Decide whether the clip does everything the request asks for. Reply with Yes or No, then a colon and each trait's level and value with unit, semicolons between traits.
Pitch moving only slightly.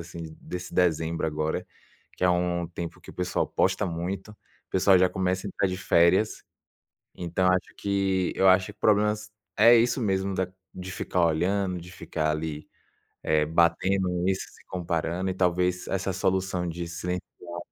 Yes: narrow, 1.9 semitones